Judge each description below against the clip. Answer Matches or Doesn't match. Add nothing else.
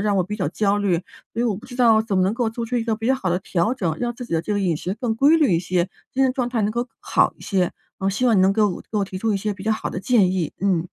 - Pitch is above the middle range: Matches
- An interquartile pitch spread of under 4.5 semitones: Matches